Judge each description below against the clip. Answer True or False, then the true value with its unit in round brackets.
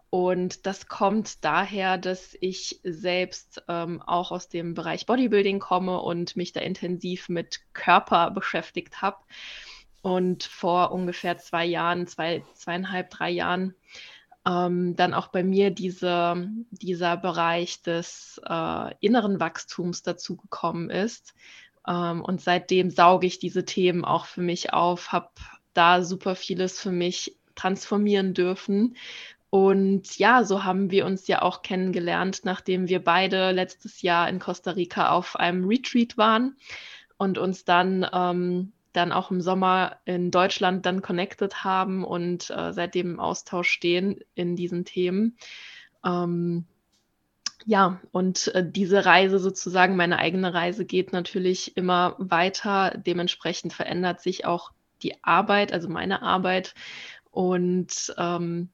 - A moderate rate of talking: True (135 wpm)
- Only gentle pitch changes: True (1.4 semitones)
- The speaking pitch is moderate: True (180 Hz)